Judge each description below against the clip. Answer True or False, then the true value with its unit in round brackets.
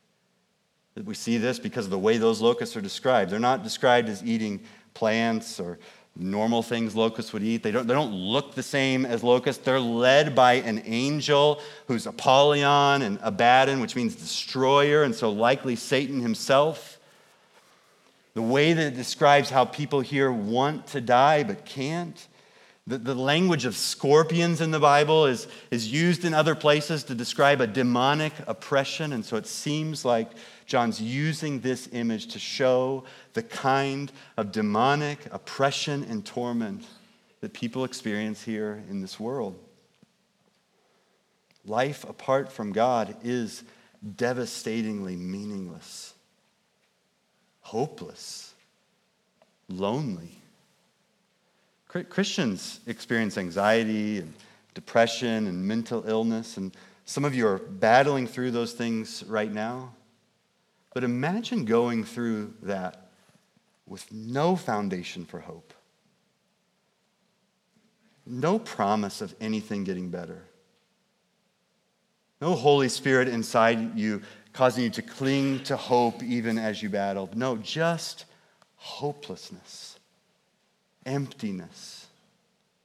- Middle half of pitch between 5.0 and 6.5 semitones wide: True (5.5 semitones)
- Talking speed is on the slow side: True (120 wpm)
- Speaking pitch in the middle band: False (130 Hz)